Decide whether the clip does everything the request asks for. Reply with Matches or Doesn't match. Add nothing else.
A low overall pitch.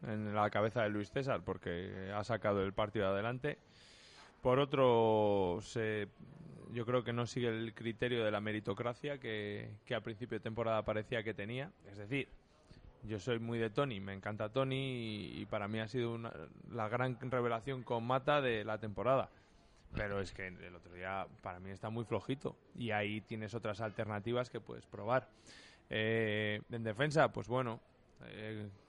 Matches